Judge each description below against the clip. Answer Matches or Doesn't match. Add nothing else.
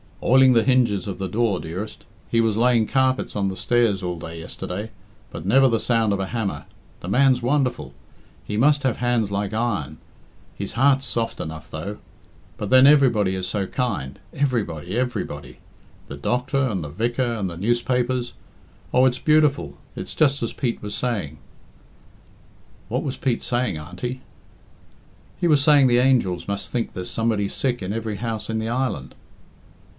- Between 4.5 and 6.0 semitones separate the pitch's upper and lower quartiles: Matches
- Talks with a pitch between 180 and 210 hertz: Doesn't match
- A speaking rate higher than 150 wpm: Matches